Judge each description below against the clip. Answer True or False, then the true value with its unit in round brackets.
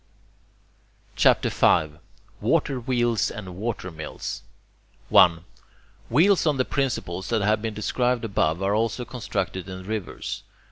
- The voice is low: True (110 Hz)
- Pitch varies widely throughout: False (4.7 semitones)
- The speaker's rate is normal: False (125 wpm)